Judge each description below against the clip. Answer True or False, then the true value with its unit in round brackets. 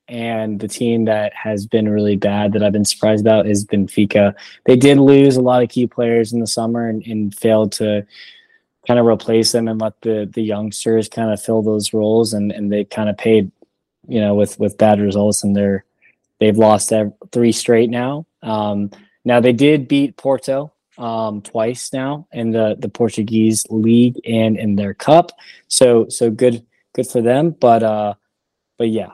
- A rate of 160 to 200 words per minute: True (190 wpm)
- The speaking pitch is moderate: False (110 Hz)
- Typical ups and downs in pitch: False (2.3 semitones)